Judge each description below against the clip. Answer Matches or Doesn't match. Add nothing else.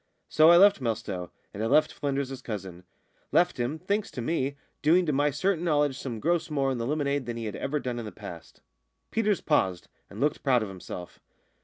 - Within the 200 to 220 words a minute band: Matches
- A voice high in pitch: Doesn't match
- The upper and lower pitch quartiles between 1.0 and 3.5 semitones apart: Doesn't match